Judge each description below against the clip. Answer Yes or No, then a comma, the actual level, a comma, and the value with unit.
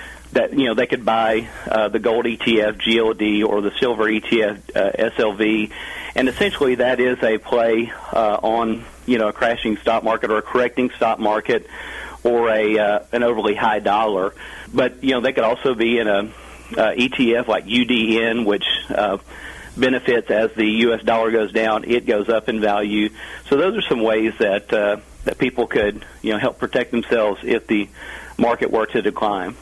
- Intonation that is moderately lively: No, narrow, 1.6 semitones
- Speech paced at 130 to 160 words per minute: No, average, 185 wpm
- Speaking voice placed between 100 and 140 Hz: Yes, low, 110 Hz